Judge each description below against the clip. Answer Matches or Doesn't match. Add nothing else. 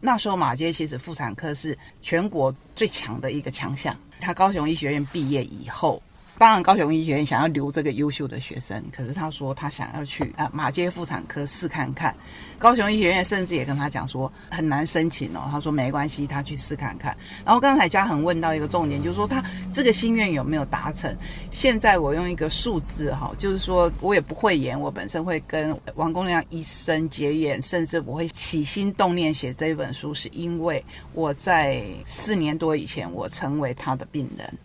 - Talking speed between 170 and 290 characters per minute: Doesn't match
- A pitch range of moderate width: Matches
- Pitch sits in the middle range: Matches